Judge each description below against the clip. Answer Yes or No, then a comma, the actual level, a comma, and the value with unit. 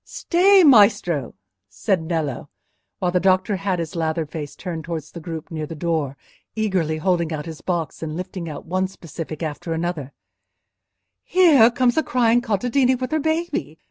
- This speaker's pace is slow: No, average, 165 wpm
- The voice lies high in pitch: No, medium, 175 Hz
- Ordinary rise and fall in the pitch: No, wide, 5.8 semitones